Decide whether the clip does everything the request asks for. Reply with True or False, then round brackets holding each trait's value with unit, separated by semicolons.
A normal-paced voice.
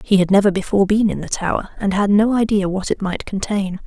False (250 wpm)